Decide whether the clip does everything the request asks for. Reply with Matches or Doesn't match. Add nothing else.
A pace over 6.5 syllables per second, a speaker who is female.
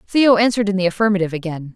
Matches